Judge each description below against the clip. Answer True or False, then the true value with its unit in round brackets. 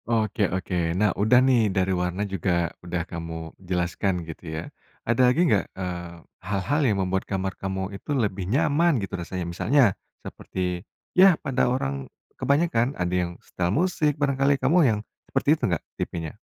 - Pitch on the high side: False (95 Hz)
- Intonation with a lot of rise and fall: True (6.1 semitones)